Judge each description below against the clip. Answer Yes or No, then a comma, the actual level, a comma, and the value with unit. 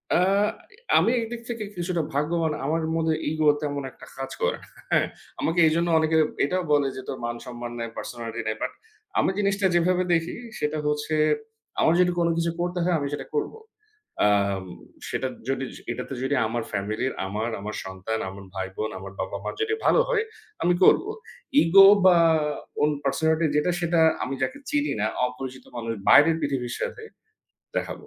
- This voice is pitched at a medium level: Yes, medium, 150 Hz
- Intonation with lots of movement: Yes, wide, 6.4 semitones